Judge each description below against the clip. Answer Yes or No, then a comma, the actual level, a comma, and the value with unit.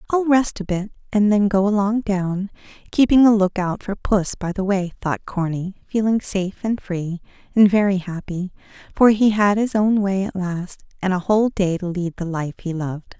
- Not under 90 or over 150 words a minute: No, fast, 205 wpm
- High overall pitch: Yes, high, 195 Hz